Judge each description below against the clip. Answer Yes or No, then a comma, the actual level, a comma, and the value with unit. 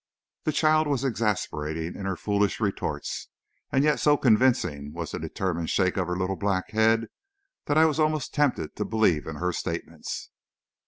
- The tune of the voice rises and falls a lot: Yes, wide, 7.4 semitones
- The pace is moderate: Yes, average, 170 wpm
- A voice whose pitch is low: Yes, low, 105 Hz